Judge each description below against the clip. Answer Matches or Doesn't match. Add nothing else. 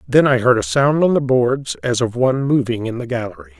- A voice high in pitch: Doesn't match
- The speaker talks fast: Matches